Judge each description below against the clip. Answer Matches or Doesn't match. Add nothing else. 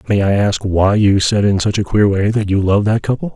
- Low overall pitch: Matches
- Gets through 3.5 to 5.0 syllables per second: Doesn't match